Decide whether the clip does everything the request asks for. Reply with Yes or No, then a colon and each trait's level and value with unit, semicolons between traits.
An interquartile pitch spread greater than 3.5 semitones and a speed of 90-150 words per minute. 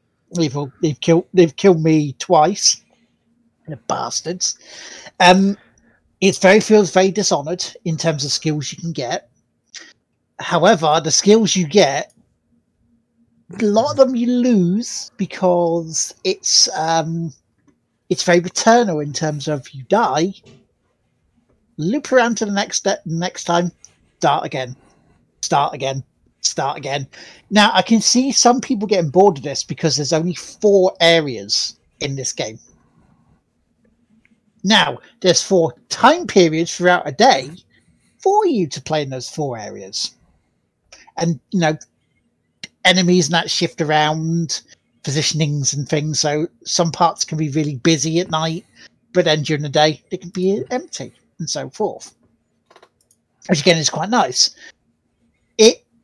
Yes: average, 4.4 semitones; average, 140 wpm